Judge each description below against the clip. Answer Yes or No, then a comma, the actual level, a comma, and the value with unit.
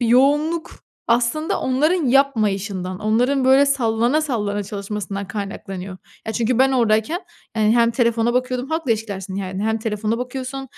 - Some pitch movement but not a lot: Yes, average, 4.1 semitones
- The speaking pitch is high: Yes, high, 230 Hz